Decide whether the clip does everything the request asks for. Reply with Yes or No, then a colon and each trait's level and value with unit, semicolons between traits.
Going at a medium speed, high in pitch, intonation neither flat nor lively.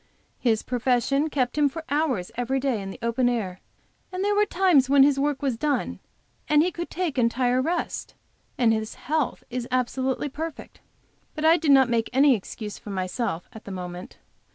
Yes: average, 180 wpm; very high, 260 Hz; average, 4.2 semitones